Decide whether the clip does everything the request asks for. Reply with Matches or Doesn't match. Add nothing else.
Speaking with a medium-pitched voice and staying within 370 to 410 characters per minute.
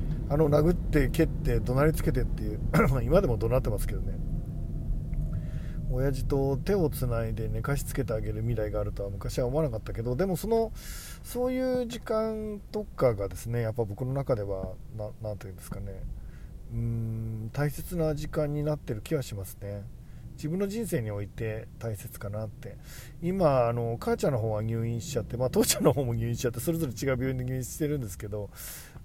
Doesn't match